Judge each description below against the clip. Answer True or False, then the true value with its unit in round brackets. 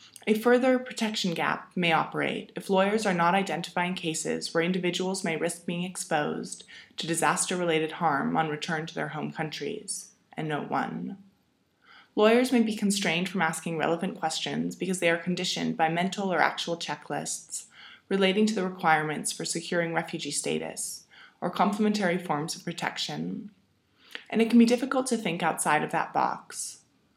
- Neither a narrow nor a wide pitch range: True (4.1 semitones)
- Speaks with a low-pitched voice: False (180 Hz)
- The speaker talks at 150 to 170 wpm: True (155 wpm)